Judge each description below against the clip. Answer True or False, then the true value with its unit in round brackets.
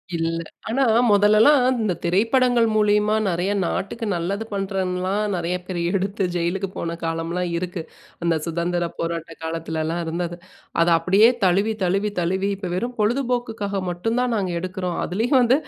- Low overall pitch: False (190 Hz)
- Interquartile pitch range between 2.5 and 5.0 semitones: True (3.7 semitones)